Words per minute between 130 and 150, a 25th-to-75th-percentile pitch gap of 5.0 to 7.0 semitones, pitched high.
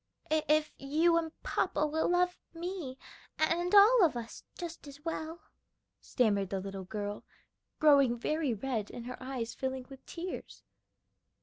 Yes: average, 140 wpm; wide, 5.6 semitones; very high, 290 Hz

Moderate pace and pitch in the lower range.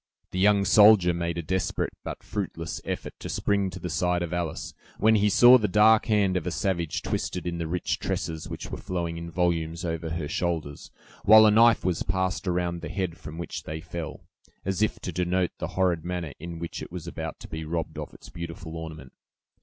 No: fast, 210 wpm; very low, 85 Hz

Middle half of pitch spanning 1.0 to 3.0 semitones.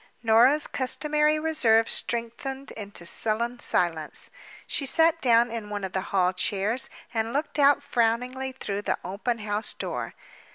No: average, 4.9 semitones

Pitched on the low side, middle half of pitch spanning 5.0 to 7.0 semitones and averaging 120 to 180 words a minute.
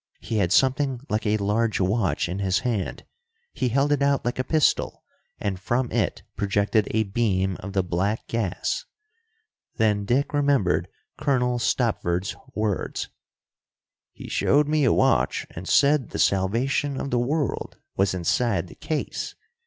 Yes: low, 110 Hz; average, 5.3 semitones; average, 150 wpm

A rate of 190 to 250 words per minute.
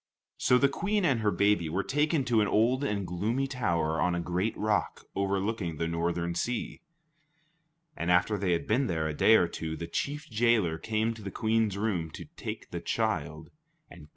Yes: average, 200 wpm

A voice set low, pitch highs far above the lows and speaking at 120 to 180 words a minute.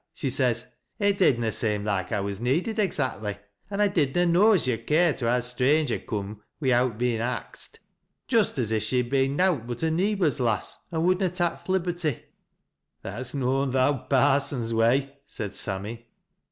No: low, 130 Hz; wide, 6.4 semitones; average, 195 wpm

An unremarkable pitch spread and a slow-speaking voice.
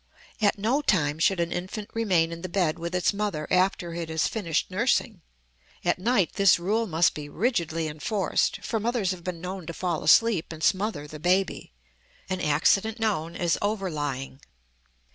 No: average, 4.1 semitones; average, 175 wpm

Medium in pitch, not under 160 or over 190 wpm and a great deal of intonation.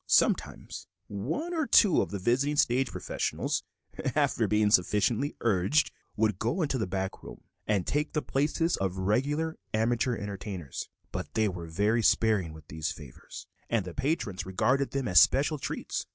No: low, 110 Hz; average, 165 wpm; wide, 6.6 semitones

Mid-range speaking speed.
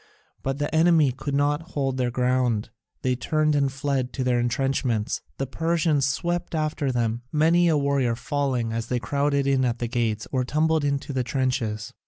Yes: average, 180 wpm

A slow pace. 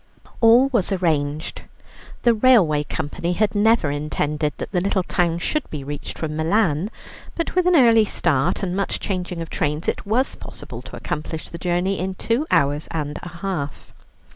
No: average, 170 wpm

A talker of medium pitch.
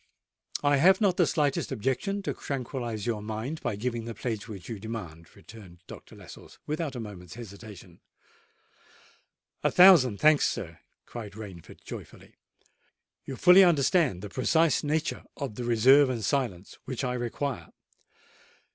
No: low, 120 Hz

